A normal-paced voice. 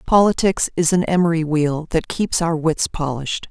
Yes: average, 170 wpm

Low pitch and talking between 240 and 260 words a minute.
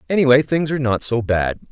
No: low, 130 Hz; fast, 210 wpm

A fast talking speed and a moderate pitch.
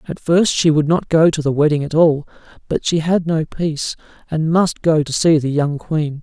Yes: fast, 230 wpm; medium, 155 Hz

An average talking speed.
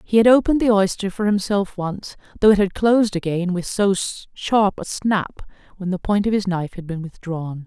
No: fast, 210 wpm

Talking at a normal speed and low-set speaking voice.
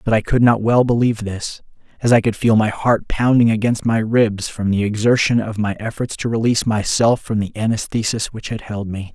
No: fast, 215 wpm; low, 110 Hz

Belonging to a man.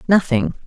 No: female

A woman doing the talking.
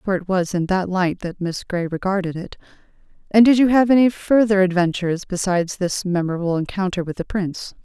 Yes: female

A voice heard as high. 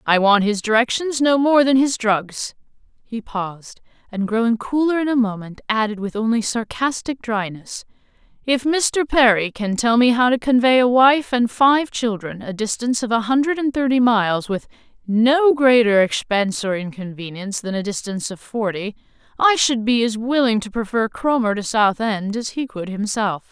Yes: high, 230 Hz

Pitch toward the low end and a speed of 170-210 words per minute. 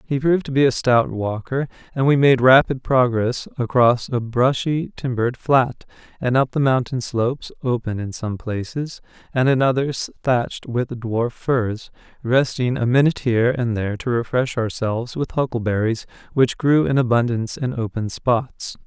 No: low, 125 Hz; average, 160 wpm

